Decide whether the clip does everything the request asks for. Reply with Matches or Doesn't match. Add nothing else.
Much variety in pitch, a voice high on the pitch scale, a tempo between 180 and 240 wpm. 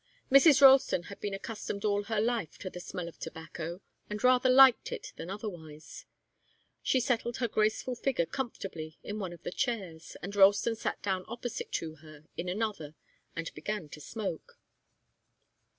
Doesn't match